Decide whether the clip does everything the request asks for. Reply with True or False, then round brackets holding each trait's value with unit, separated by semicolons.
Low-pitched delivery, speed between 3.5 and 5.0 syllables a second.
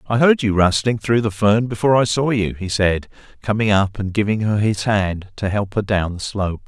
False (105 Hz; 5.2 syllables/s)